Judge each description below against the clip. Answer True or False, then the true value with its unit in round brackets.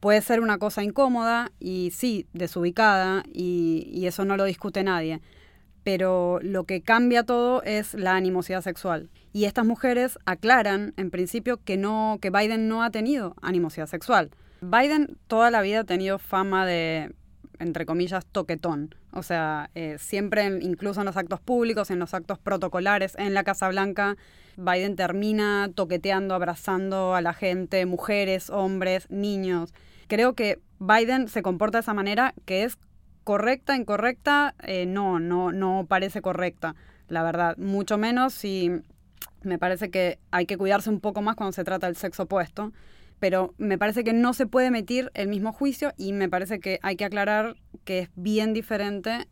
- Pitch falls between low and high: False (195 Hz)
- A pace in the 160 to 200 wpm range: True (170 wpm)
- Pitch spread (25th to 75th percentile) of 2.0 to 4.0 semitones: True (2.9 semitones)